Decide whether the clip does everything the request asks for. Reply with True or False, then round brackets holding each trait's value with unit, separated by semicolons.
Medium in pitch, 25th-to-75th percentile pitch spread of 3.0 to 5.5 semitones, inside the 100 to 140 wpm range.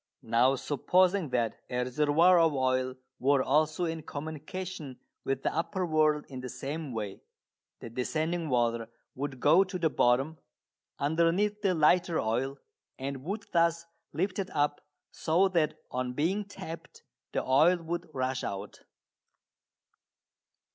True (155 Hz; 4.8 semitones; 135 wpm)